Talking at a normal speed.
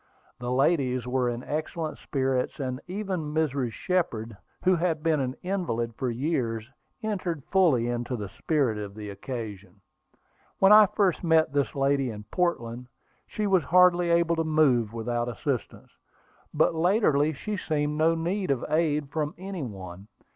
Yes: average, 155 wpm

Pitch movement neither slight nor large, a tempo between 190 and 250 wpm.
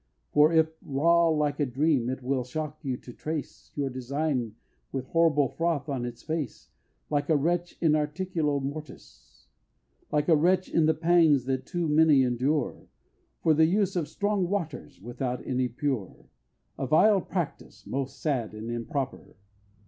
No: average, 3.7 semitones; average, 160 wpm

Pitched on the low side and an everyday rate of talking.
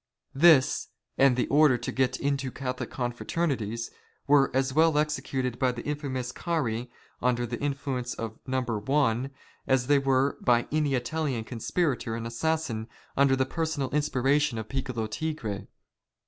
Yes: low, 130 Hz; average, 145 wpm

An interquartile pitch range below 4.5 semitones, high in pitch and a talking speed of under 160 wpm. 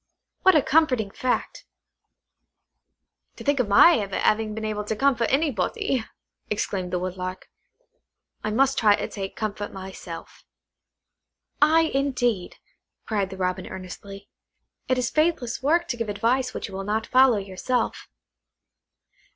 No: average, 5.1 semitones; high, 220 Hz; slow, 135 wpm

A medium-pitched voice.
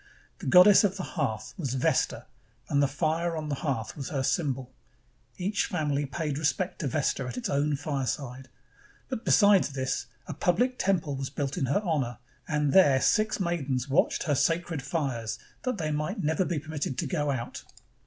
Yes: medium, 150 Hz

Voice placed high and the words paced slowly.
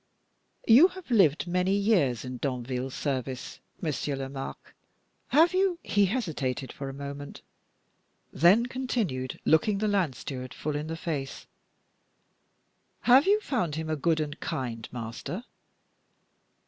No: medium, 155 Hz; slow, 130 wpm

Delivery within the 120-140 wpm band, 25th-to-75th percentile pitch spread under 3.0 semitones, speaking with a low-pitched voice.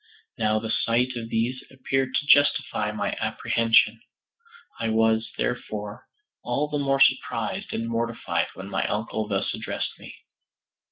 Yes: slow, 135 wpm; narrow, 2.6 semitones; low, 115 Hz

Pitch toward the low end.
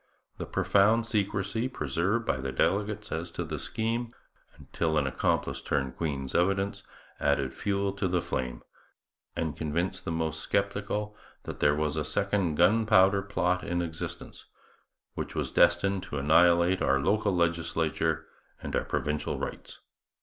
Yes: very low, 85 Hz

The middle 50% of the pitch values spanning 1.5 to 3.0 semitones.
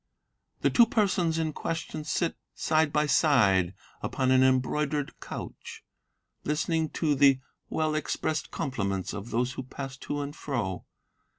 No: average, 3.4 semitones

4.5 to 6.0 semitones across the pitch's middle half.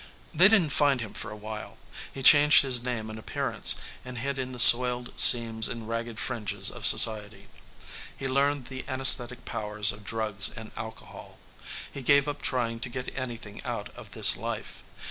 No: average, 3.3 semitones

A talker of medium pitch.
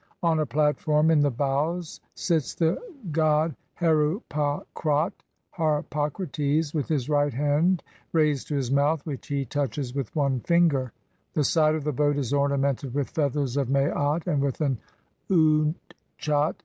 Yes: medium, 150 Hz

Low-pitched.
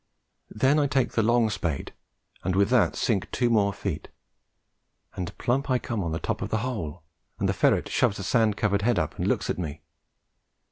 Yes: low, 105 Hz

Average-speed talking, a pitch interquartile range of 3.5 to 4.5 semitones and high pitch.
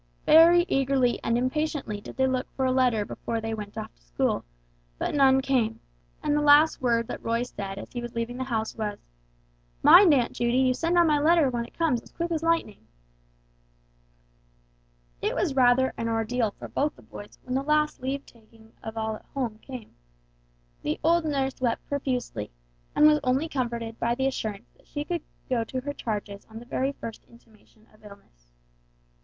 Yes: average, 195 wpm; average, 4.0 semitones; high, 245 Hz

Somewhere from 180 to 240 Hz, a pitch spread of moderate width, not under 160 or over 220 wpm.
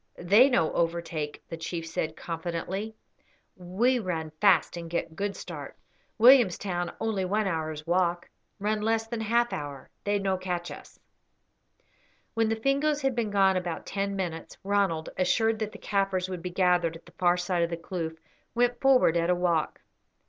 Yes: medium, 185 Hz; average, 4.2 semitones; average, 170 wpm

